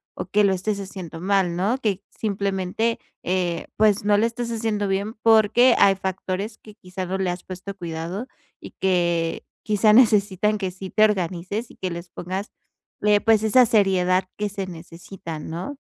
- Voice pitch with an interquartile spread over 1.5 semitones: Yes, average, 2.7 semitones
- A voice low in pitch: No, high, 195 Hz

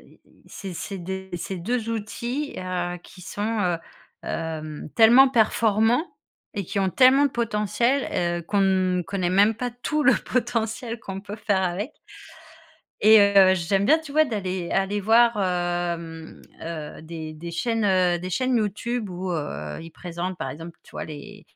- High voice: Yes, high, 195 Hz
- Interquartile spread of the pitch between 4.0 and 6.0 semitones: Yes, average, 4.7 semitones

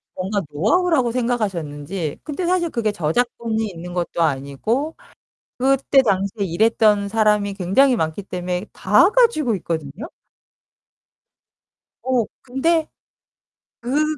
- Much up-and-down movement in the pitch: Yes, wide, 6.7 semitones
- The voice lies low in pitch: No, high, 215 Hz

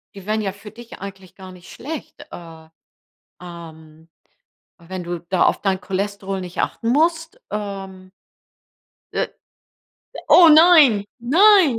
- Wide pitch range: Yes, wide, 6.7 semitones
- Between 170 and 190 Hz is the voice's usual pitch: No, high, 200 Hz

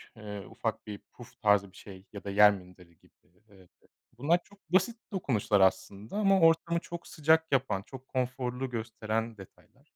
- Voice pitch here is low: Yes, low, 115 Hz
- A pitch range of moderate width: No, wide, 8.0 semitones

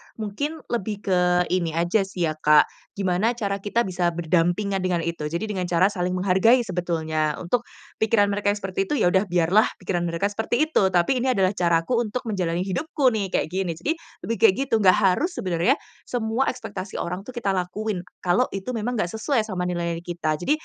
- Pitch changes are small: No, average, 3.9 semitones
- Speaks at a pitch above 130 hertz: Yes, high, 190 Hz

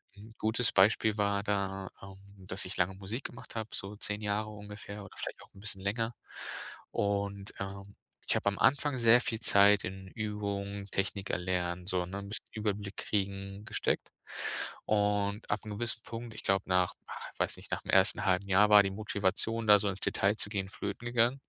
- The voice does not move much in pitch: Yes, narrow, 1.7 semitones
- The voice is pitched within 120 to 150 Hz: No, low, 100 Hz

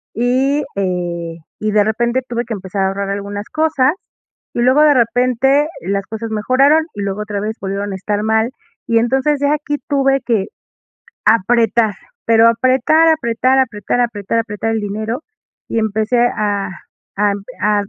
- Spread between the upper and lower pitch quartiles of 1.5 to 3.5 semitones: No, average, 4.0 semitones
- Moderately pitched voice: No, high, 225 Hz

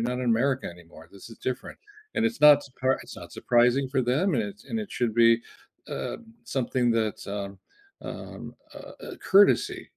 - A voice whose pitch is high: No, low, 125 Hz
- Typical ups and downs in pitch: Yes, average, 3.6 semitones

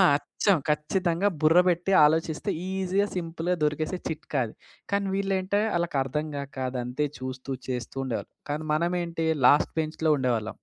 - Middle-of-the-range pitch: Yes, medium, 160 Hz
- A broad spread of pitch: No, average, 4.0 semitones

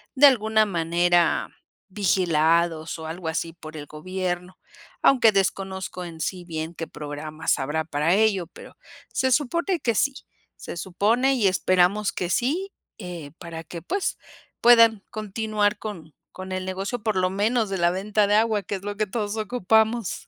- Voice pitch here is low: No, high, 190 Hz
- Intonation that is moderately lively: Yes, average, 4.3 semitones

